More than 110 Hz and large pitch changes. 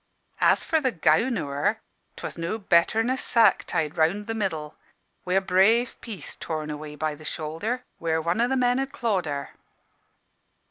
Yes: medium, 185 Hz; wide, 6.6 semitones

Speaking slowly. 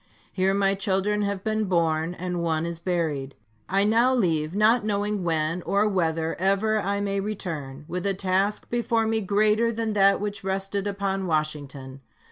No: average, 165 wpm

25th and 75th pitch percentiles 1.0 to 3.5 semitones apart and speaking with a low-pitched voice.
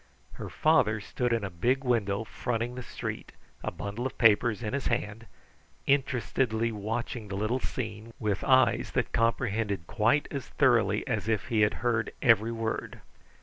Yes: narrow, 2.6 semitones; low, 115 Hz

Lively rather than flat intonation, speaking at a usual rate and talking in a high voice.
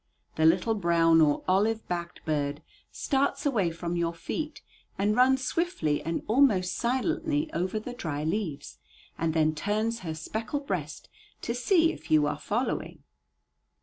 Yes: wide, 7.4 semitones; average, 150 wpm; high, 195 Hz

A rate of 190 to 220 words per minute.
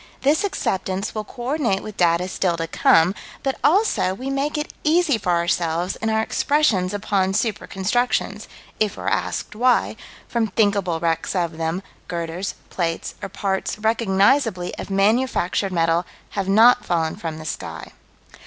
No: average, 155 wpm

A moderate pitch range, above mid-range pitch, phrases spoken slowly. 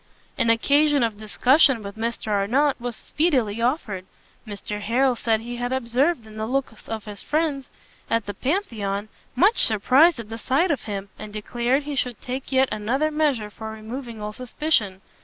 No: average, 4.1 semitones; high, 235 Hz; average, 175 wpm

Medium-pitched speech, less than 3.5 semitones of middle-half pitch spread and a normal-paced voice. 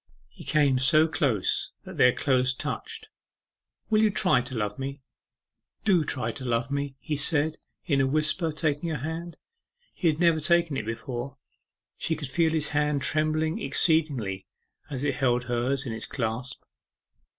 No: medium, 145 Hz; average, 3.8 semitones; average, 160 wpm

